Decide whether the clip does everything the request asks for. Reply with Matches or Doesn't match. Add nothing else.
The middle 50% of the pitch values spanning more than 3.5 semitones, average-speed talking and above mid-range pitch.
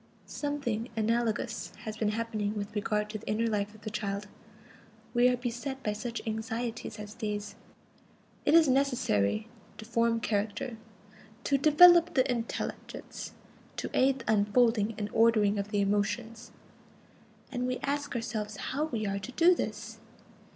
Doesn't match